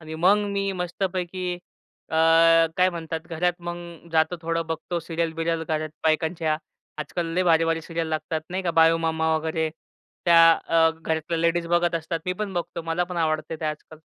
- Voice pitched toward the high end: No, medium, 165 Hz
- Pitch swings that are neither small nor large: No, narrow, 1.5 semitones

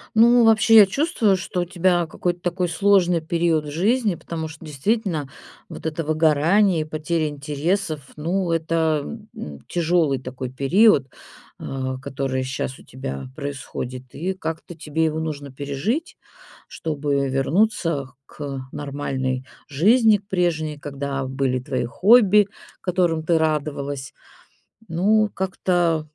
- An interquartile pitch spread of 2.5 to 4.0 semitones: No, average, 4.6 semitones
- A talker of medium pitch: Yes, medium, 160 Hz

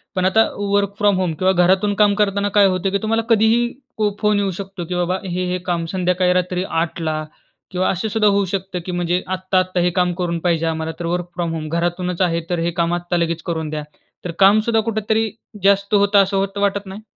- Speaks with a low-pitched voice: No, medium, 185 Hz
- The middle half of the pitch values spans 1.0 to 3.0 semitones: Yes, narrow, 2.6 semitones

